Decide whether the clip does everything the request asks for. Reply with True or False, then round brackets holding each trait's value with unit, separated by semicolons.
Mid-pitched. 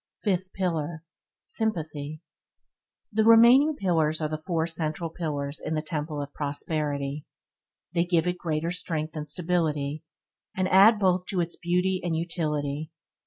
True (165 Hz)